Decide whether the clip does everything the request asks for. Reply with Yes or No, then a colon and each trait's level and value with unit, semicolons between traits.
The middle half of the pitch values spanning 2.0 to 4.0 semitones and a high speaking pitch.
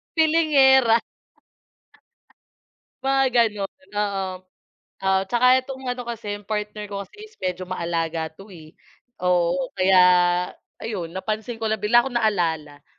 No: average, 4.6 semitones; high, 210 Hz